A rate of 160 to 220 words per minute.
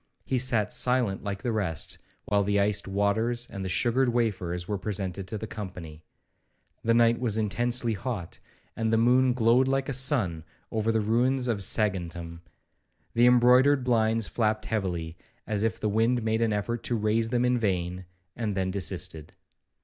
Yes: average, 170 wpm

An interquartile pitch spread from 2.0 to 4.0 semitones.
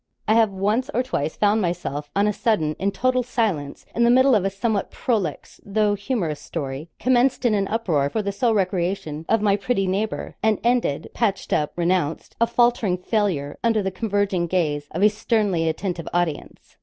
No: average, 4.6 semitones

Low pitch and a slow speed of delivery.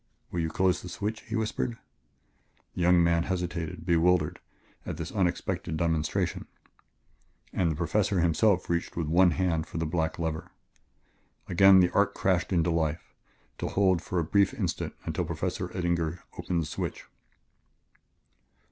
No: very low, 85 Hz; average, 150 wpm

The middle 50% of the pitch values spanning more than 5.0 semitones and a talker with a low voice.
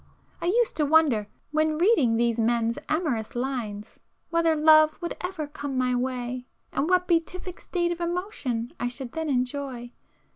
No: wide, 5.6 semitones; very high, 285 Hz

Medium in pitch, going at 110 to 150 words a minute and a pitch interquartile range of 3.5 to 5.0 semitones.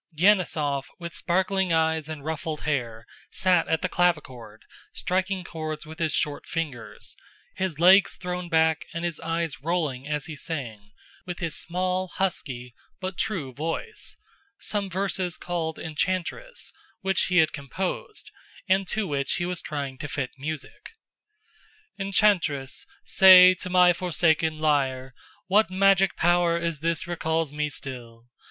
Yes: medium, 165 Hz; average, 140 wpm; average, 3.8 semitones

